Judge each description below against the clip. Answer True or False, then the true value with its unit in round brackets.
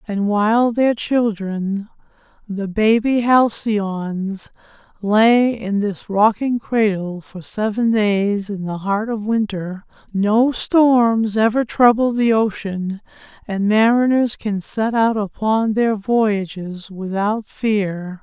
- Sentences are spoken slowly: True (120 wpm)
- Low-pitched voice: False (215 Hz)